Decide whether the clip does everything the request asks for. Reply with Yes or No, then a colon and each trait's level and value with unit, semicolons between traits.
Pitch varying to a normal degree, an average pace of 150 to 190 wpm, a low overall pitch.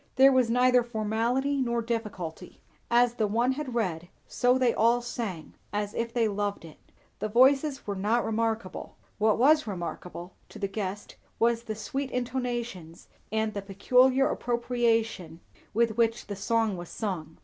No: average, 3.2 semitones; average, 155 wpm; high, 230 Hz